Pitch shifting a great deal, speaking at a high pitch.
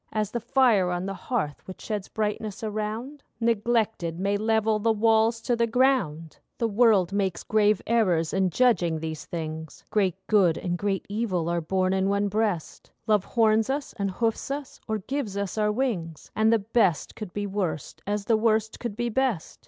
No: average, 3.4 semitones; high, 210 Hz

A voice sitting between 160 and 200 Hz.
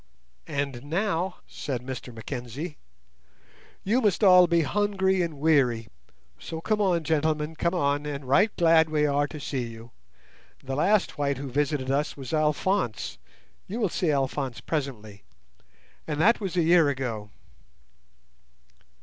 No: medium, 150 Hz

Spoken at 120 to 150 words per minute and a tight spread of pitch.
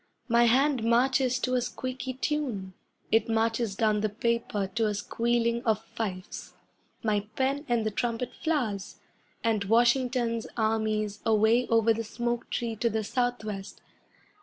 Yes: average, 140 wpm; narrow, 2.2 semitones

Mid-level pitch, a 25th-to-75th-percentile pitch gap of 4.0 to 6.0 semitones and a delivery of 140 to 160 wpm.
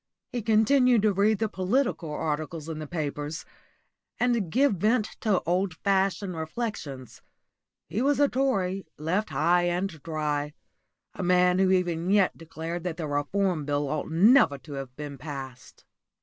Yes: medium, 175 Hz; average, 5.1 semitones; average, 150 wpm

